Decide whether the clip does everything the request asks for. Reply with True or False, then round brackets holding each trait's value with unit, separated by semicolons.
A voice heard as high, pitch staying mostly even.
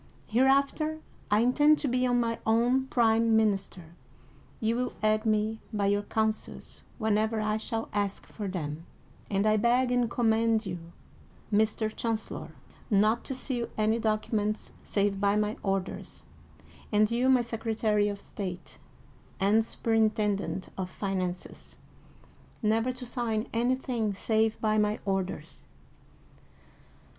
True (220 Hz; 2.2 semitones)